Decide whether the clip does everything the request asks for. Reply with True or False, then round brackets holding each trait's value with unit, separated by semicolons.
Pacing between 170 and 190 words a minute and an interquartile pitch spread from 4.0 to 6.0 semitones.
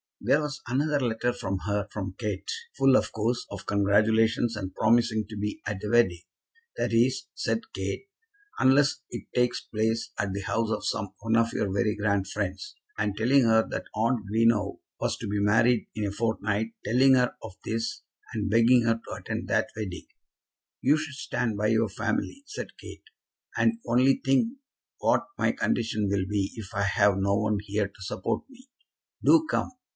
False (180 wpm; 3.0 semitones)